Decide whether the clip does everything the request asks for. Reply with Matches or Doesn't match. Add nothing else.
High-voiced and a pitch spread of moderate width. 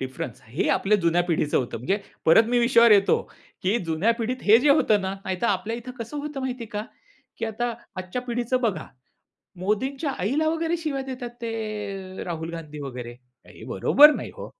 Doesn't match